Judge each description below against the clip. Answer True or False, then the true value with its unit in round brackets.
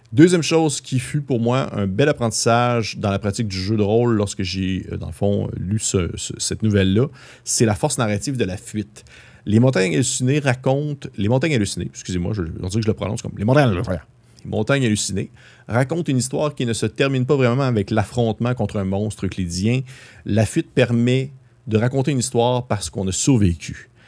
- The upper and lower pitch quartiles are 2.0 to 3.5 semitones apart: False (4.1 semitones)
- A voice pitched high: False (115 Hz)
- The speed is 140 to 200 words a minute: True (195 wpm)